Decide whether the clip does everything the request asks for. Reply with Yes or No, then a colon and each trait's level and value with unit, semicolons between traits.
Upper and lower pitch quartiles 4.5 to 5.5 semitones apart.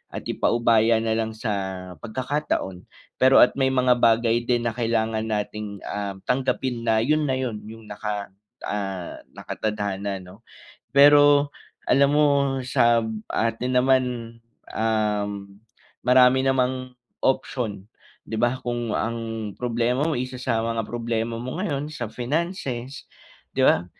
No: average, 2.8 semitones